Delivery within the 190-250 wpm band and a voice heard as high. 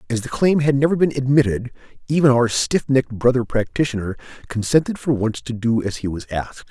No: average, 195 wpm; low, 125 Hz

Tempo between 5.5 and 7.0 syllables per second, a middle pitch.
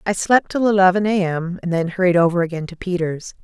Yes: 5.9 syllables/s; medium, 180 Hz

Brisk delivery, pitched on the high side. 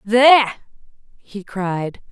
No: slow, 85 wpm; high, 215 Hz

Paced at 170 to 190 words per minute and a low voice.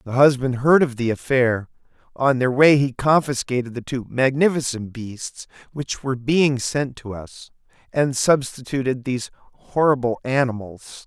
No: average, 140 wpm; low, 130 Hz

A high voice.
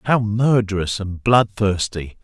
No: low, 105 Hz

